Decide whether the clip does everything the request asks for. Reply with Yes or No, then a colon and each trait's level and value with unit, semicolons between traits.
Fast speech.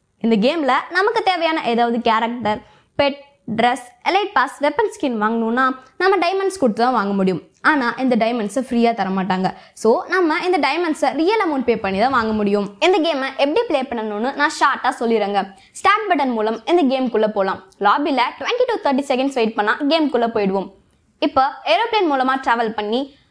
Yes: fast, 160 wpm